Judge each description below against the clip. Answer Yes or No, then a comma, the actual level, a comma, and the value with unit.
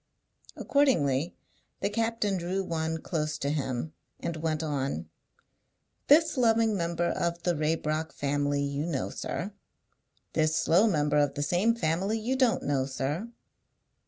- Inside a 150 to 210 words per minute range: No, slow, 135 wpm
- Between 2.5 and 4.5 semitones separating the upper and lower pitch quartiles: No, wide, 5.6 semitones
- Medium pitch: Yes, medium, 160 Hz